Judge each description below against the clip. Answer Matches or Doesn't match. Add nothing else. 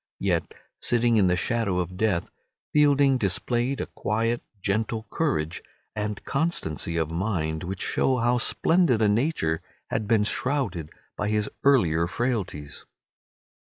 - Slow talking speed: Matches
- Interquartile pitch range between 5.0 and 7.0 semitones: Matches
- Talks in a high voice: Doesn't match